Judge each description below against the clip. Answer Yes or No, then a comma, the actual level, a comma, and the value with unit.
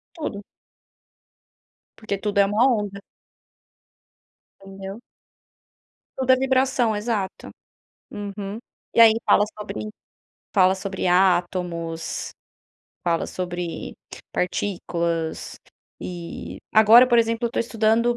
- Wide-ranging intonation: No, average, 4.0 semitones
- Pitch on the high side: Yes, high, 200 Hz